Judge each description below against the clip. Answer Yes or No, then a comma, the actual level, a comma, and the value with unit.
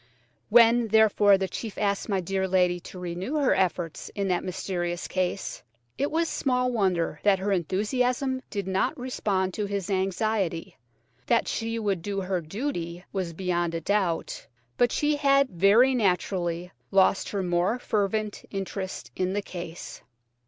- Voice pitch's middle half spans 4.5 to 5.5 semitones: No, average, 3.5 semitones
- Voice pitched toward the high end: Yes, high, 195 Hz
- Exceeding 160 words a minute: No, average, 150 wpm